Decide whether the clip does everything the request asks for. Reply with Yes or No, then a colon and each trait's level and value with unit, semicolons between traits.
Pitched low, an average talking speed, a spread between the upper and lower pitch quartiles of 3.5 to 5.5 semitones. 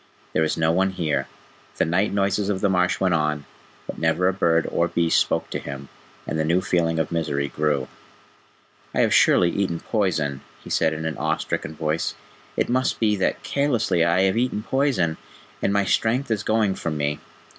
Yes: very low, 85 Hz; average, 195 wpm; average, 4.0 semitones